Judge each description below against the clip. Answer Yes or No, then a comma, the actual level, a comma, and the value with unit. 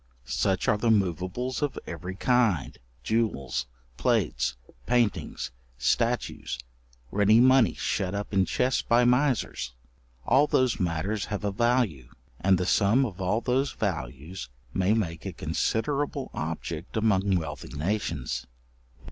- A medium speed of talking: No, slow, 125 wpm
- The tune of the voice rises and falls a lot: Yes, wide, 6.0 semitones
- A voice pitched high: No, low, 100 Hz